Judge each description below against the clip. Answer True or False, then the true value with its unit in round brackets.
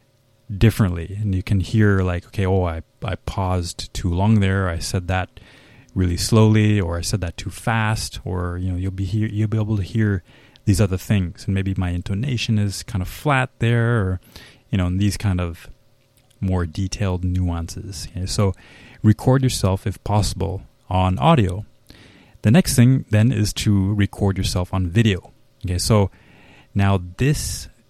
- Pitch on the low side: True (100 Hz)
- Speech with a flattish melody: False (3.3 semitones)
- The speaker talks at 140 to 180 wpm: True (170 wpm)